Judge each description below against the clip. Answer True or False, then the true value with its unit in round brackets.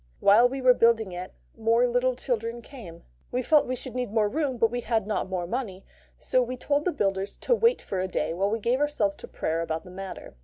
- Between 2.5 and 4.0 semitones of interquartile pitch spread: False (4.6 semitones)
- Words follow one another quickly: True (230 wpm)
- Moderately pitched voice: False (230 Hz)